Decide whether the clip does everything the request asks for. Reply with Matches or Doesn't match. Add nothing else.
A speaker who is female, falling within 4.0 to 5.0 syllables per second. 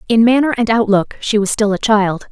Doesn't match